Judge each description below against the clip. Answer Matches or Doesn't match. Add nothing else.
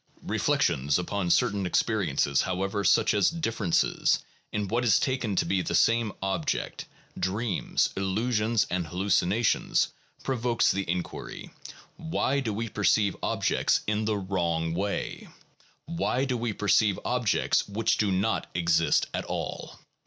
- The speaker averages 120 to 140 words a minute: Matches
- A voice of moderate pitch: Doesn't match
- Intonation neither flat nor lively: Matches